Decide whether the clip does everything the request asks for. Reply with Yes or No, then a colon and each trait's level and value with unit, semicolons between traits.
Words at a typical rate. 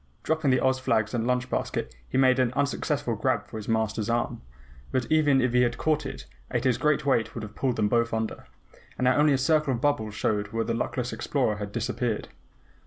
No: fast, 215 wpm